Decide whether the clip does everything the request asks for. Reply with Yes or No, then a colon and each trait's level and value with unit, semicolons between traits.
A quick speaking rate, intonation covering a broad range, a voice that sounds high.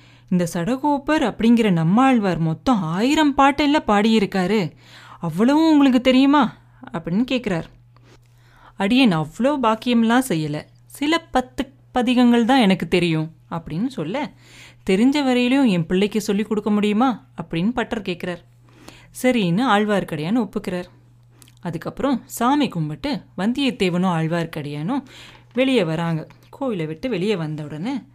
No: average, 105 wpm; wide, 7.4 semitones; high, 205 Hz